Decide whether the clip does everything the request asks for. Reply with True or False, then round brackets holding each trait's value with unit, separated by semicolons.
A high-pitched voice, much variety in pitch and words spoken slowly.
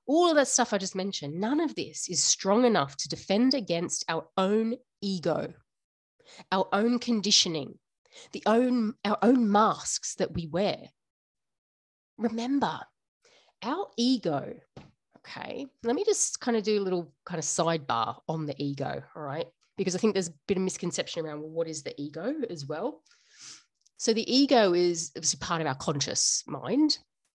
False (195 Hz; 6.5 semitones; 165 wpm)